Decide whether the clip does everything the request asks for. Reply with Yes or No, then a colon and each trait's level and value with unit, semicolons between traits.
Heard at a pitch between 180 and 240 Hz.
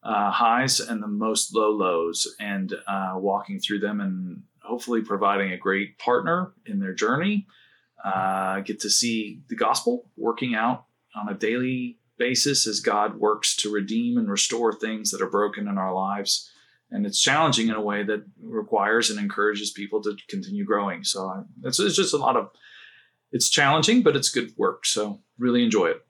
No: low, 110 Hz